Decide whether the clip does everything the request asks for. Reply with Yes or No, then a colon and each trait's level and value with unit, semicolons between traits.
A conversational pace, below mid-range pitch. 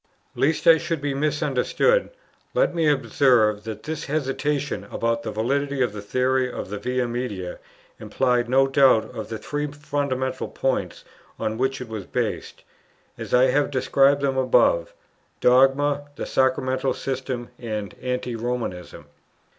Yes: average, 145 wpm; low, 130 Hz